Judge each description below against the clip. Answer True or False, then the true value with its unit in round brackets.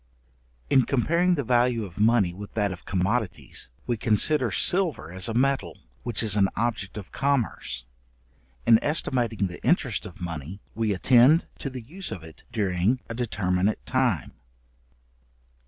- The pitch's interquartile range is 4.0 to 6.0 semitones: True (5.1 semitones)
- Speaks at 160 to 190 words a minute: False (150 wpm)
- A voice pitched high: False (110 Hz)